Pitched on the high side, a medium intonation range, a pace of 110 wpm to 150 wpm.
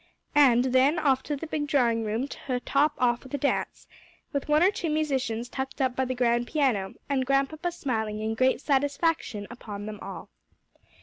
No: very high, 265 Hz; average, 3.4 semitones; average, 185 wpm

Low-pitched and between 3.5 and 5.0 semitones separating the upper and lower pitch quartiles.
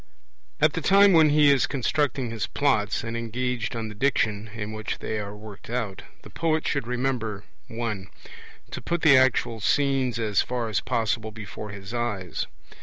Yes: low, 115 Hz; average, 4.1 semitones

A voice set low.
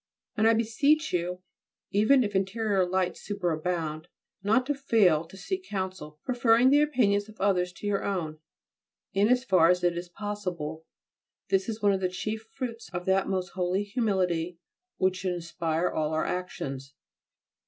No: high, 190 Hz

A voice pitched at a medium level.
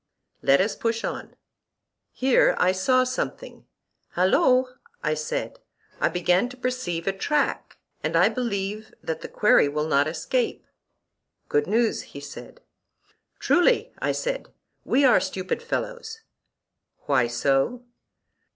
No: high, 220 Hz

